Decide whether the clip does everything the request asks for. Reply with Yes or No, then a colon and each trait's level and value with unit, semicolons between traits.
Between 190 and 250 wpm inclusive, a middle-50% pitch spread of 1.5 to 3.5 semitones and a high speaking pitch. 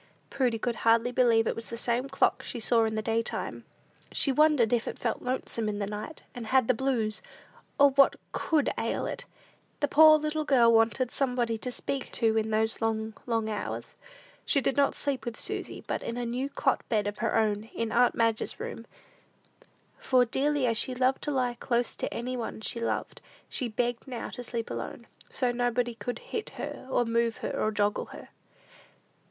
Yes: average, 195 wpm; narrow, 2.5 semitones; high, 240 Hz